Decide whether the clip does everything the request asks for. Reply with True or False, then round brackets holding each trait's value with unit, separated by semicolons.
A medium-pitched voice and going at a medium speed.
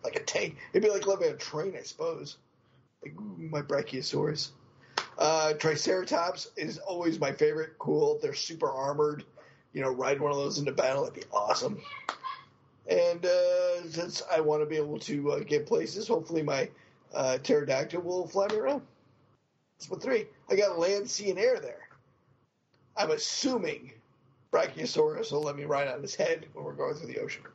True (180 Hz; 175 wpm)